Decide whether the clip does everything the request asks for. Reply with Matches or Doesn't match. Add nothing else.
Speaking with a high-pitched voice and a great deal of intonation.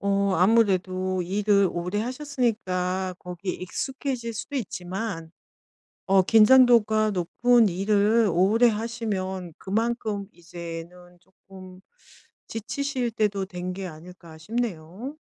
Doesn't match